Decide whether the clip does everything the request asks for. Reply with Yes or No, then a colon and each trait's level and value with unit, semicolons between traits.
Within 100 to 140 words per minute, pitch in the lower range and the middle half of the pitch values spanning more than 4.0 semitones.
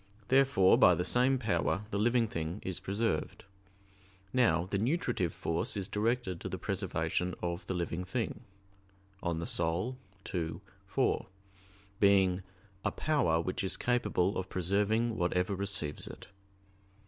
Yes: slow, 135 wpm; very low, 95 Hz; average, 4.5 semitones